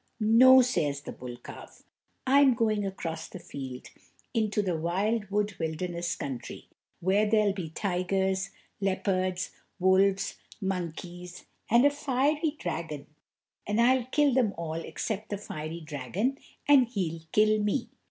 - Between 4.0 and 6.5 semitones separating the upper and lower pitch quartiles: Yes, average, 4.8 semitones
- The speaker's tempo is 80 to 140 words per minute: Yes, slow, 135 wpm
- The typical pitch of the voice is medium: No, high, 195 Hz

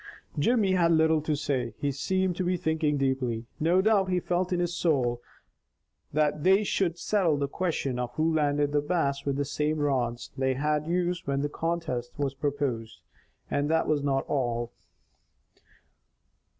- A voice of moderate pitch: Yes, medium, 150 Hz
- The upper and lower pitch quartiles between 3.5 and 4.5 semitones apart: Yes, average, 3.9 semitones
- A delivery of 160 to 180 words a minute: Yes, average, 165 wpm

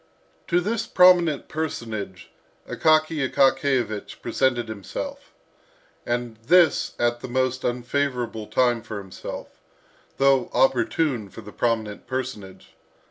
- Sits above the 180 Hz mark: No, low, 125 Hz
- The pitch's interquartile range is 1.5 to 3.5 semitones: No, average, 4.0 semitones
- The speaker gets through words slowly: Yes, slow, 105 wpm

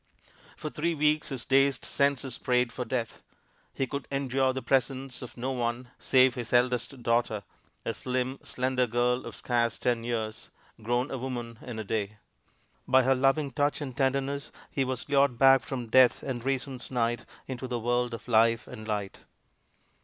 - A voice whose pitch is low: Yes, low, 125 Hz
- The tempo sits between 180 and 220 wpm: No, average, 170 wpm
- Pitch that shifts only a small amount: Yes, narrow, 2.0 semitones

